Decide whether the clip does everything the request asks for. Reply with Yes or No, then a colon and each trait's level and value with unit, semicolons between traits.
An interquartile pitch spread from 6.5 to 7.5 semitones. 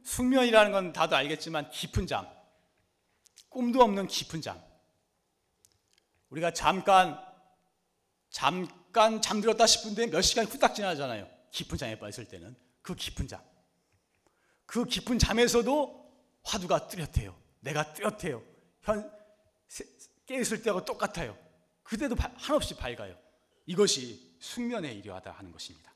Yes: wide, 7.1 semitones